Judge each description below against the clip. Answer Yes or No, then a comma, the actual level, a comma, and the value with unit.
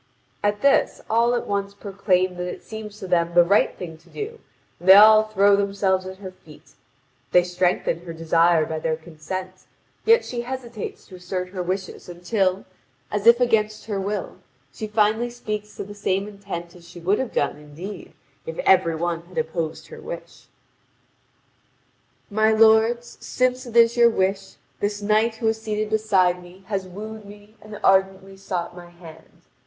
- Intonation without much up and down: No, average, 3.4 semitones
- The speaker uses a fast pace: No, average, 175 wpm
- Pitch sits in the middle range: No, high, 195 Hz